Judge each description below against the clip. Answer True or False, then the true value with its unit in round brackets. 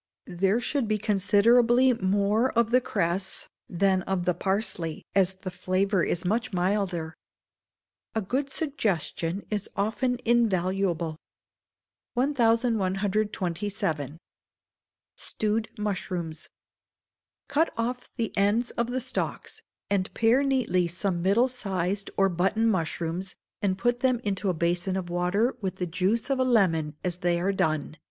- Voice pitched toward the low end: False (195 Hz)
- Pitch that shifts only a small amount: False (4.2 semitones)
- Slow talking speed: True (130 wpm)